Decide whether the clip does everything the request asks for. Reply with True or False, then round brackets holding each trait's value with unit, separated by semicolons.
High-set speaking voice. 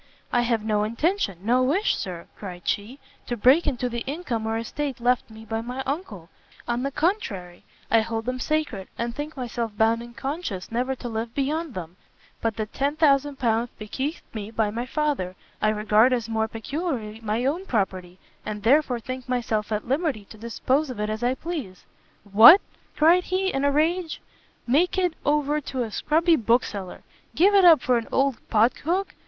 True (245 Hz)